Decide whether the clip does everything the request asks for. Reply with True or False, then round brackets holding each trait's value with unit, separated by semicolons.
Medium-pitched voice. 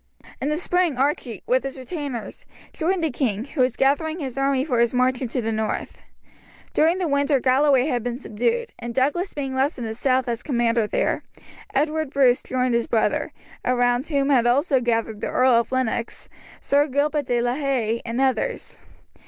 False (260 Hz)